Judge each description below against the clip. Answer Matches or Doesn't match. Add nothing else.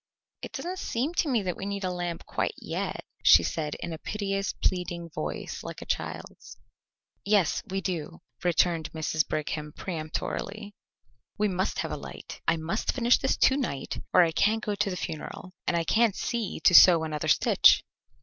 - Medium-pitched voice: Matches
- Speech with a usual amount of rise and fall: Matches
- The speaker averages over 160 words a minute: Matches